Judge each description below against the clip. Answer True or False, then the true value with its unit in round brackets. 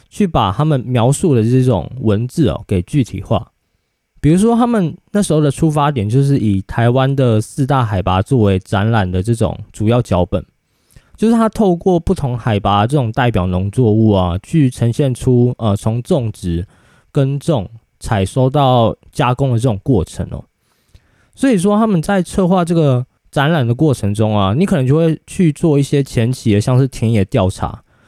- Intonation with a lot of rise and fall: True (5.9 semitones)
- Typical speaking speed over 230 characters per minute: True (265 characters per minute)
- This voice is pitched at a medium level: False (125 Hz)